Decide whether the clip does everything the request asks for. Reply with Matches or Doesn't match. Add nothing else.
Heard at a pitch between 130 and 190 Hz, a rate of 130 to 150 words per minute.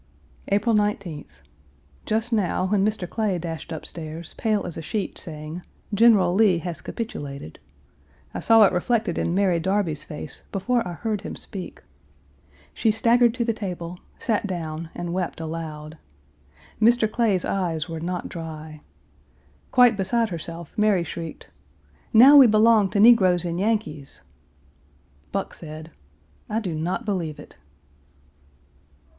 Matches